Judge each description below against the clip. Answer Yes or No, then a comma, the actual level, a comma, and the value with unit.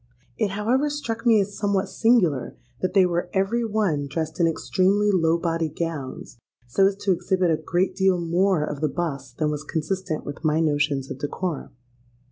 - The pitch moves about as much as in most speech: Yes, average, 4.3 semitones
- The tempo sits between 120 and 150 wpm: No, average, 180 wpm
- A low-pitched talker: No, medium, 175 Hz